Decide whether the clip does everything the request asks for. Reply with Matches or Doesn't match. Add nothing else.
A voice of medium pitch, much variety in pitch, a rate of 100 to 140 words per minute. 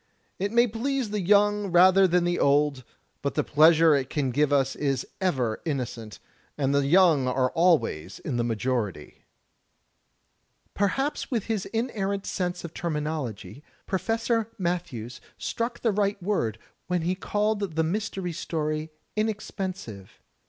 Matches